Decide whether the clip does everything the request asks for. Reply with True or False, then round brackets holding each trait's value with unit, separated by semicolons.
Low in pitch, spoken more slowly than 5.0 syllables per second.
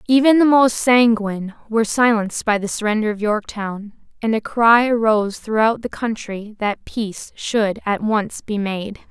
False (220 Hz; 4.7 syllables/s)